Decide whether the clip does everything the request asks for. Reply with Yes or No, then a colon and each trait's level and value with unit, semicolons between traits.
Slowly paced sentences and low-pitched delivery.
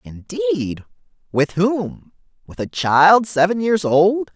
No: slow, 110 wpm; medium, 175 Hz